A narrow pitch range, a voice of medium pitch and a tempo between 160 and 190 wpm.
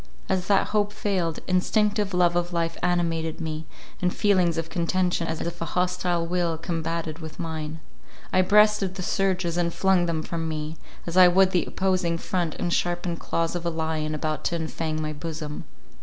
Yes: narrow, 2.1 semitones; medium, 170 Hz; average, 180 wpm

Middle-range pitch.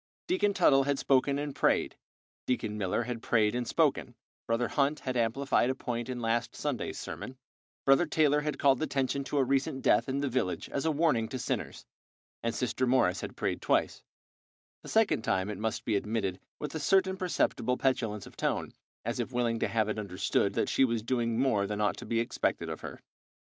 No: low, 125 Hz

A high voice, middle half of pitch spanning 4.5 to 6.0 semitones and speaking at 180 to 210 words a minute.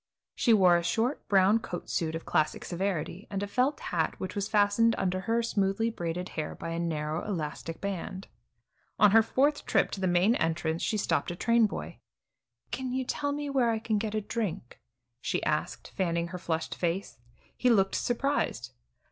Yes: high, 195 Hz; average, 5.0 semitones; average, 185 wpm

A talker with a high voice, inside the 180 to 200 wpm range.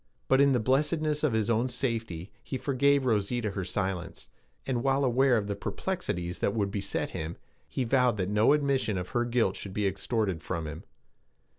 No: low, 115 Hz; average, 185 wpm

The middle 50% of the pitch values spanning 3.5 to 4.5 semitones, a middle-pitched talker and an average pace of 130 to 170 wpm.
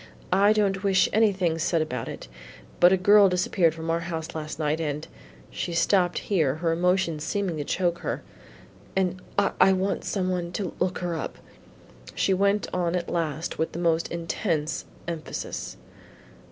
No: average, 2.8 semitones; medium, 175 Hz; average, 165 wpm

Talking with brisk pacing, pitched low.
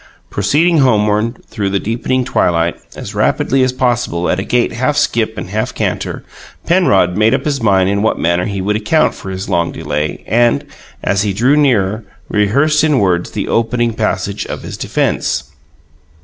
No: average, 175 wpm; low, 110 Hz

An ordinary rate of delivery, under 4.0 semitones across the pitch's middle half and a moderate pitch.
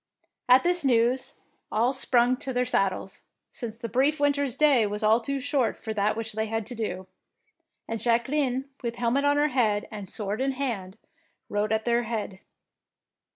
No: average, 175 wpm; average, 3.5 semitones; high, 235 Hz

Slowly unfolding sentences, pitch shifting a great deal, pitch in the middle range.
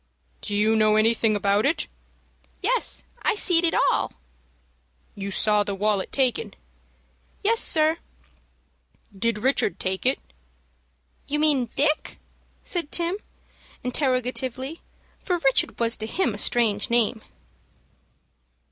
No: slow, 115 wpm; wide, 6.4 semitones; high, 245 Hz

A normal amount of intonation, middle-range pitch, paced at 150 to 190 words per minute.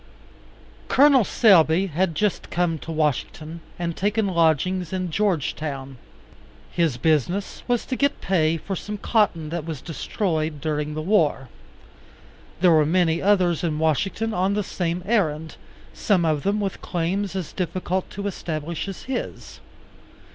No: average, 3.9 semitones; medium, 175 Hz; average, 140 wpm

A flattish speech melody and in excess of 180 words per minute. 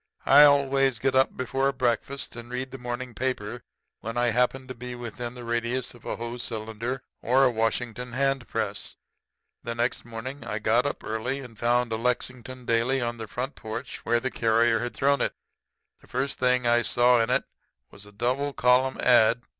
Yes: narrow, 1.8 semitones; average, 190 wpm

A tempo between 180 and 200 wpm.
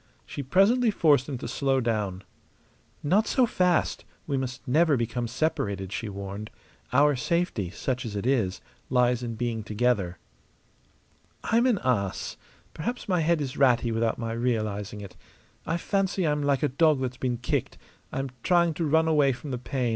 No: average, 170 wpm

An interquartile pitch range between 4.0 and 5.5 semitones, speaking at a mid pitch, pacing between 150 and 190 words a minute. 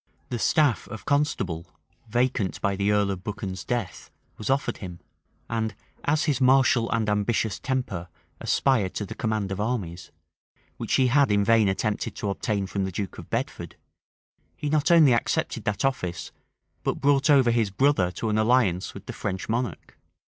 No: average, 4.7 semitones; low, 110 Hz; average, 170 wpm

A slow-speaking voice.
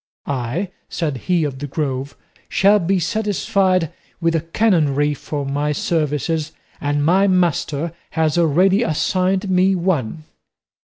Yes: slow, 125 wpm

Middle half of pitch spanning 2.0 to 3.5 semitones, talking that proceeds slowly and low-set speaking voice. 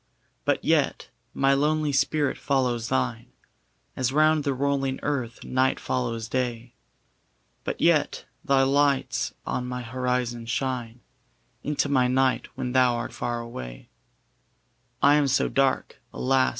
Yes: narrow, 2.4 semitones; slow, 130 wpm; low, 130 Hz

